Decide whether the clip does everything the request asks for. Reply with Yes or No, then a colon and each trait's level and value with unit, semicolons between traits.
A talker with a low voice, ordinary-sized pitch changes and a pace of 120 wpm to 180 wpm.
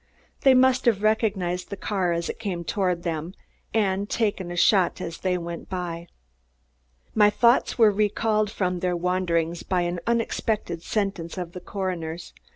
No: medium, 185 Hz; average, 3.3 semitones; average, 160 wpm